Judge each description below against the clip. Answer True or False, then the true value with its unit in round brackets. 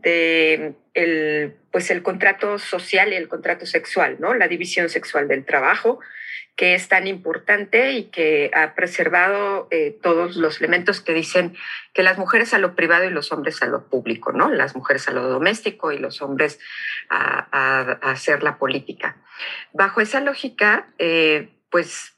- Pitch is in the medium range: True (180 Hz)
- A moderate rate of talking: True (170 wpm)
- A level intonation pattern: False (3.9 semitones)